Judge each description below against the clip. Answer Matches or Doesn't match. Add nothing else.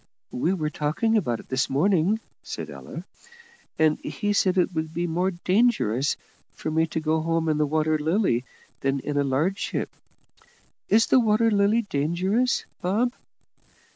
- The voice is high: Doesn't match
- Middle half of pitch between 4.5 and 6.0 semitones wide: Matches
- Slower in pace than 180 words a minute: Matches